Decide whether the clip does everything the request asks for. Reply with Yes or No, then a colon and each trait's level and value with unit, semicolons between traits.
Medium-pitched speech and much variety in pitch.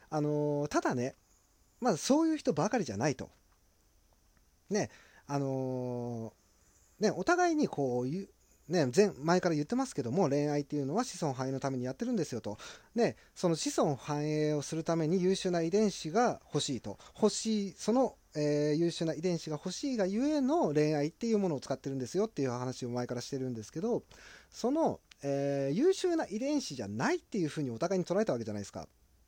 Yes: medium, 150 Hz; wide, 7.5 semitones